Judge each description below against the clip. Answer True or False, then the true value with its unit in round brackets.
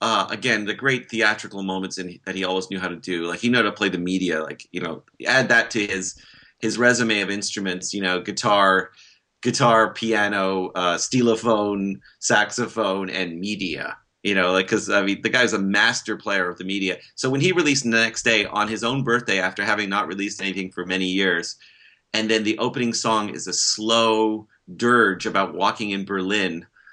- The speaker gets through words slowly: False (195 wpm)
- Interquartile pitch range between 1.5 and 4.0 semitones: True (3.1 semitones)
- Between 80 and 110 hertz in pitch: True (100 Hz)